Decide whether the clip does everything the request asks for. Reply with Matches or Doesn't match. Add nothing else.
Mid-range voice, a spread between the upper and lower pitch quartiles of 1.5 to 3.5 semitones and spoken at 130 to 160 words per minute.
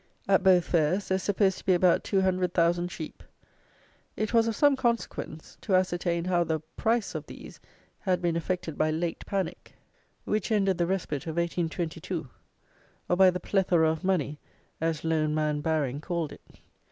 Doesn't match